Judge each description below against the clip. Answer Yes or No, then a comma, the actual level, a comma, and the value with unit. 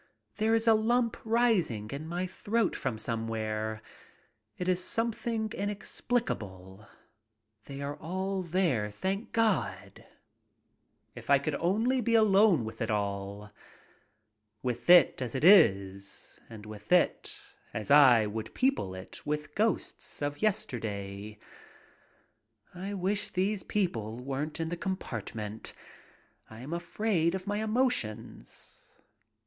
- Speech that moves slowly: Yes, slow, 120 wpm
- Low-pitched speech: No, medium, 155 Hz